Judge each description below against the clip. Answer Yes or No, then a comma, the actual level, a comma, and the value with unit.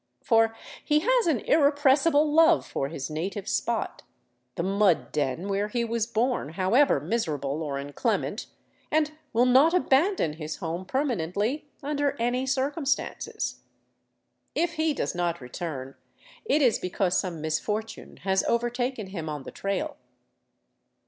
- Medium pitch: No, high, 225 Hz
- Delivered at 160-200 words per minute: No, slow, 135 wpm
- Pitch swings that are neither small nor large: No, wide, 8.6 semitones